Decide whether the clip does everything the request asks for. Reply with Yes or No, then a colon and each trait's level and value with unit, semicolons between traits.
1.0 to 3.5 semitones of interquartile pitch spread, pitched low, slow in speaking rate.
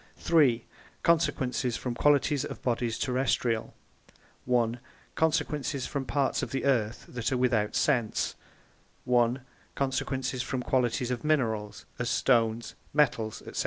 Yes: narrow, 2.6 semitones; low, 125 Hz; slow, 125 wpm